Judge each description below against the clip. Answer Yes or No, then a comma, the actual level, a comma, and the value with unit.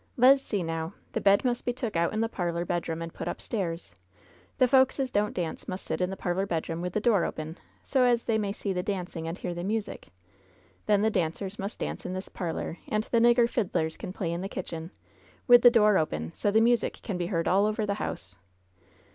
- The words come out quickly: Yes, fast, 225 wpm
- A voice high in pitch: Yes, high, 195 Hz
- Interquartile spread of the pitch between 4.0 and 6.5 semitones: Yes, average, 4.7 semitones